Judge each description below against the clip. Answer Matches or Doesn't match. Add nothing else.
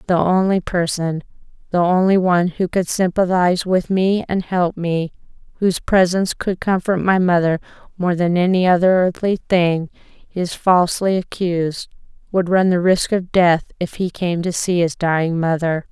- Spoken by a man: Doesn't match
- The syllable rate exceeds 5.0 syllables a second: Doesn't match